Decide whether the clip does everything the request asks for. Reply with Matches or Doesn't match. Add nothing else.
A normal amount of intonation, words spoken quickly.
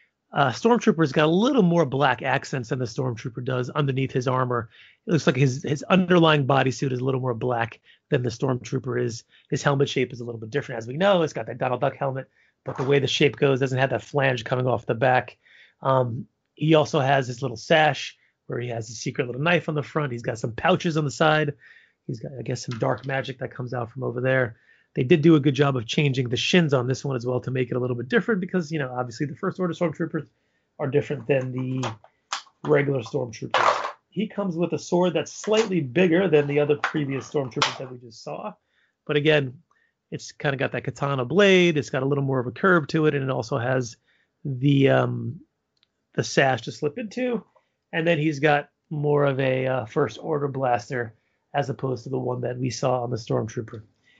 Matches